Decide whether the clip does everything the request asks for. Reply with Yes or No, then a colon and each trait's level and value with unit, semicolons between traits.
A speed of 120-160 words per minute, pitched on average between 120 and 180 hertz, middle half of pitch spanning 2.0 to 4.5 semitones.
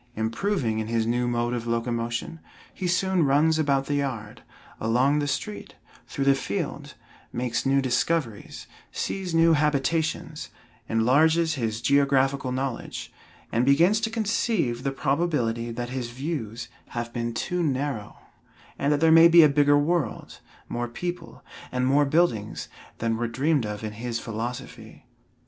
No: average, 145 wpm; low, 135 Hz; average, 5.2 semitones